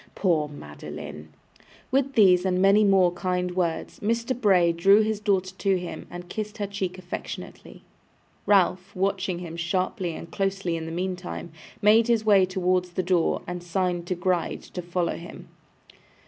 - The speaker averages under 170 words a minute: Yes, average, 160 wpm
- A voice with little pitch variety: Yes, narrow, 2.2 semitones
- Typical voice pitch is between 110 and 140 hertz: No, medium, 185 Hz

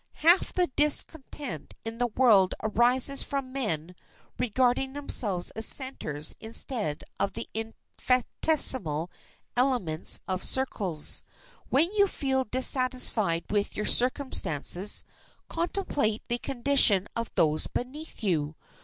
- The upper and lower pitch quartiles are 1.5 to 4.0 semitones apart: No, wide, 5.5 semitones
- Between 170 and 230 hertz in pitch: No, high, 245 Hz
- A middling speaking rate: No, slow, 110 wpm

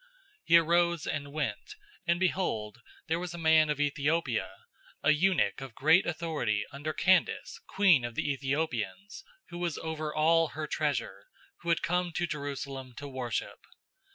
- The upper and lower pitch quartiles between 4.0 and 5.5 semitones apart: No, average, 3.6 semitones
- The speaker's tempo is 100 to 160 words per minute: Yes, average, 155 wpm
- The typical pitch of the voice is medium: Yes, medium, 155 Hz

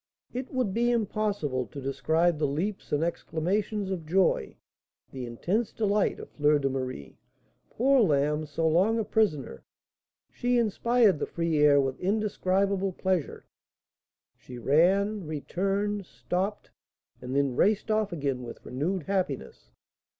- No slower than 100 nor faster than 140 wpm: Yes, slow, 135 wpm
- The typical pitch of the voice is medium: Yes, medium, 180 Hz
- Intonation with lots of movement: Yes, wide, 6.3 semitones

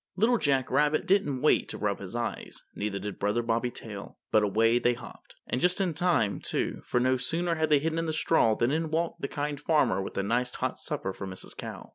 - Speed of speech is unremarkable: No, fast, 230 wpm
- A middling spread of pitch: No, wide, 6.3 semitones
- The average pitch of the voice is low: Yes, low, 130 Hz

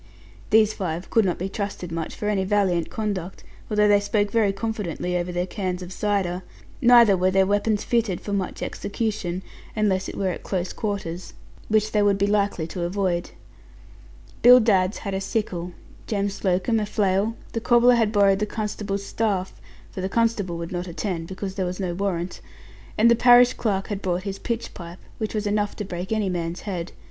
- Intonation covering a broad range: No, average, 2.7 semitones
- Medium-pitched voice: No, high, 200 Hz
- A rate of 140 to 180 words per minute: No, average, 190 wpm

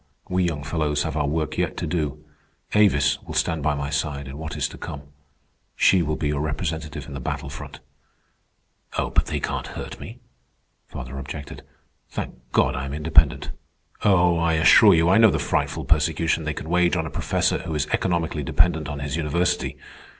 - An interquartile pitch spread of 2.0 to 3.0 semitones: Yes, narrow, 2.4 semitones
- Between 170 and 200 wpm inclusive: Yes, average, 185 wpm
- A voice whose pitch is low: Yes, very low, 75 Hz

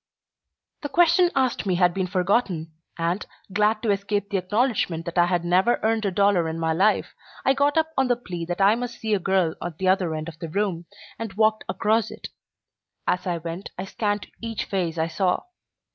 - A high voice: Yes, high, 195 Hz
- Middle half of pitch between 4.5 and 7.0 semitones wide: No, average, 4.1 semitones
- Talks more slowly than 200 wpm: No, fast, 205 wpm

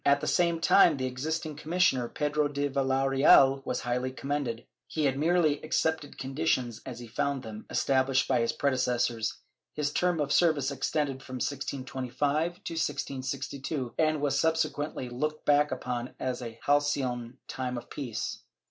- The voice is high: No, low, 135 Hz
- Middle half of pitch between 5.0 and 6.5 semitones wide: No, average, 2.7 semitones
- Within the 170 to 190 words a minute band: No, average, 150 wpm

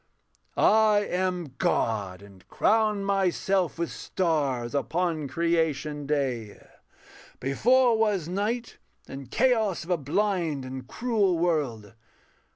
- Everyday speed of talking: No, slow, 105 wpm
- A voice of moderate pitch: Yes, medium, 170 Hz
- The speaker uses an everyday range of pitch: No, wide, 6.7 semitones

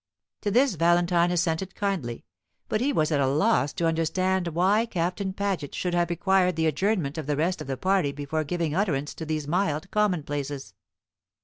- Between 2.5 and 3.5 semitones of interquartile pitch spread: No, average, 4.0 semitones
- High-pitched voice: No, medium, 170 Hz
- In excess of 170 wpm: Yes, average, 180 wpm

